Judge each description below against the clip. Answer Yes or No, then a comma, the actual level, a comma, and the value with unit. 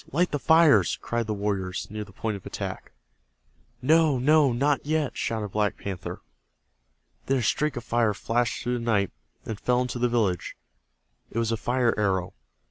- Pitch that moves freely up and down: No, average, 4.1 semitones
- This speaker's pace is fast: No, average, 175 wpm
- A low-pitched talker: Yes, low, 120 Hz